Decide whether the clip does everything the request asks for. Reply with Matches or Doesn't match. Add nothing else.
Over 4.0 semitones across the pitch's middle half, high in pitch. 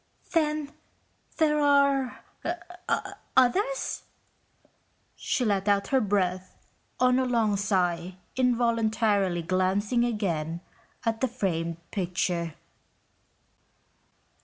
Matches